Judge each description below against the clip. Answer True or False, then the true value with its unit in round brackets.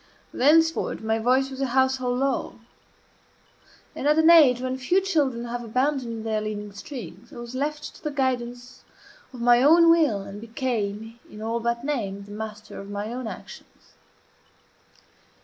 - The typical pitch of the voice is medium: False (245 Hz)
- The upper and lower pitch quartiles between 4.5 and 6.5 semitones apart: False (3.7 semitones)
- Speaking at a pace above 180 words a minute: False (160 wpm)